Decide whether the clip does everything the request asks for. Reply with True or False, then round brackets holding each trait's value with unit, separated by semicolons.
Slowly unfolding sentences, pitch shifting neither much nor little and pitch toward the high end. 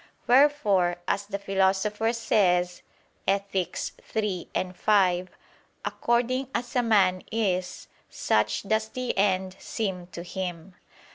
True (110 wpm; 3.4 semitones; 195 Hz)